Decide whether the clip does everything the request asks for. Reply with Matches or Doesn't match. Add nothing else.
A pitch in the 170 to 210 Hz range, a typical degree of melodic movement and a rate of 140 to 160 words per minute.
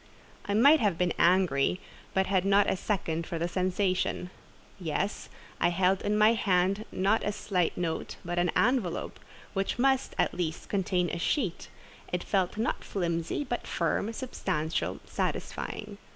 Matches